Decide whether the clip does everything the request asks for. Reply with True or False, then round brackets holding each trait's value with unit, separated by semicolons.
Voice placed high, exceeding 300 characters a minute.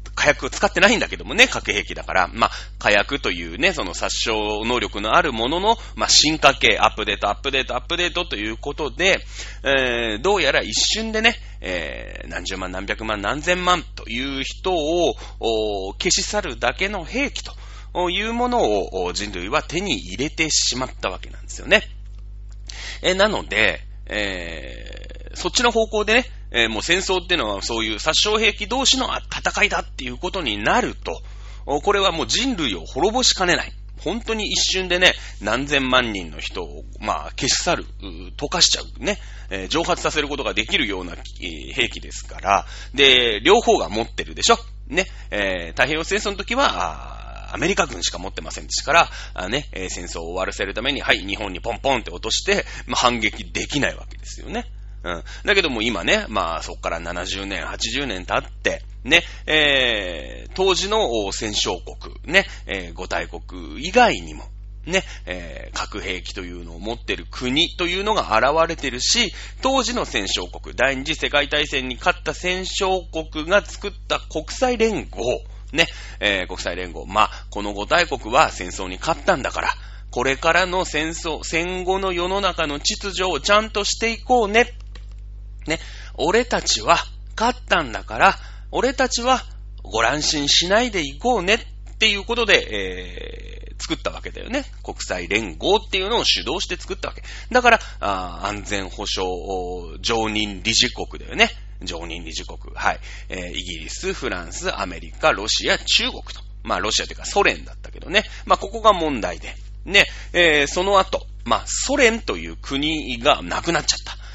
False (135 Hz; 330 characters per minute)